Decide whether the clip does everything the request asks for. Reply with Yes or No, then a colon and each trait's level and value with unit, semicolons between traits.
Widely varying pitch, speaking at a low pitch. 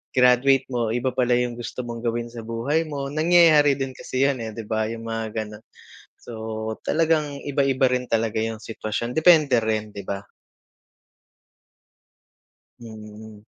No: average, 3.7 semitones; low, 120 Hz